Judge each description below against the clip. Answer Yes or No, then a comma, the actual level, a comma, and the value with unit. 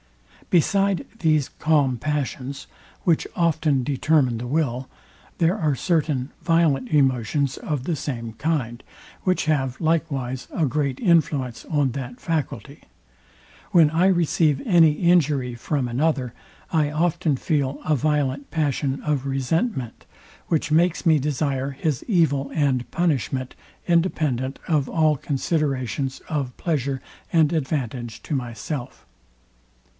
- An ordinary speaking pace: No, slow, 120 wpm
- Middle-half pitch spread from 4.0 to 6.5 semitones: No, average, 3.6 semitones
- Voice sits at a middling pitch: Yes, medium, 145 Hz